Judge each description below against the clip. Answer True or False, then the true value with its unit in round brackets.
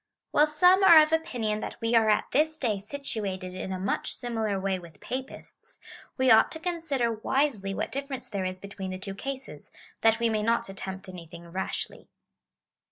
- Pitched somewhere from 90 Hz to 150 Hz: False (225 Hz)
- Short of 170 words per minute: False (180 wpm)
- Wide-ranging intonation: True (6.1 semitones)